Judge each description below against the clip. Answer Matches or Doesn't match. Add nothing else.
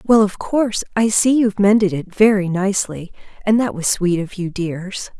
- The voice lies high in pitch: Matches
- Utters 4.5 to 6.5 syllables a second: Matches